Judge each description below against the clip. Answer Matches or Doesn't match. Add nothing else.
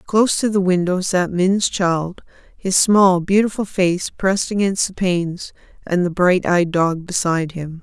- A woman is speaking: Matches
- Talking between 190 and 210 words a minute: Doesn't match